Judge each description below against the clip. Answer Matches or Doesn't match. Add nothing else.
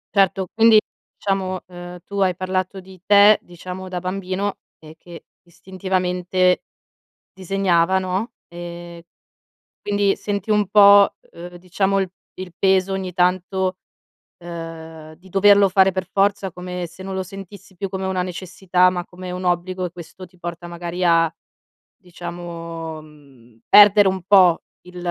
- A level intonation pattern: Matches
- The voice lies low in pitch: Doesn't match